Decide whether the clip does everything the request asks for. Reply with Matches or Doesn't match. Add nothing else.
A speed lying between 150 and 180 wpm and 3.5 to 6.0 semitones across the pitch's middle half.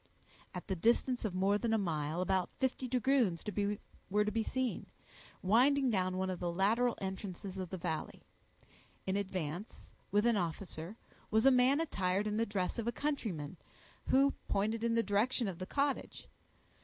Matches